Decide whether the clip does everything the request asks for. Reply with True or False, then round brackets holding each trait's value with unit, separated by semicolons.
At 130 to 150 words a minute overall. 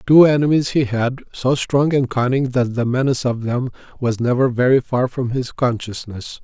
False (185 wpm)